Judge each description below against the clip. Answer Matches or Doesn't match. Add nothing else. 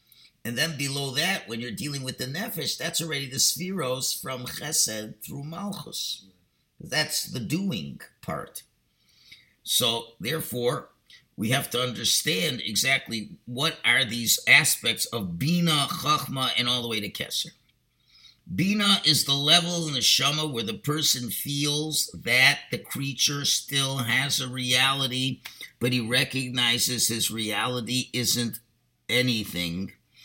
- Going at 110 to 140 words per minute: Matches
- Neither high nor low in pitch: Doesn't match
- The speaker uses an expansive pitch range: Doesn't match